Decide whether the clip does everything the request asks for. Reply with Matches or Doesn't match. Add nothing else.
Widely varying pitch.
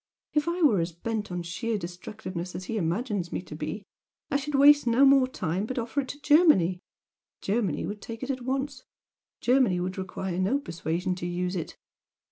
Matches